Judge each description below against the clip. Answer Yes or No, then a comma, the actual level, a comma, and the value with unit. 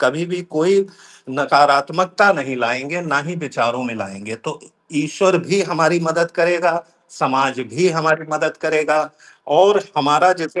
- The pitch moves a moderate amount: Yes, average, 3.8 semitones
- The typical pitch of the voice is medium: Yes, medium, 160 Hz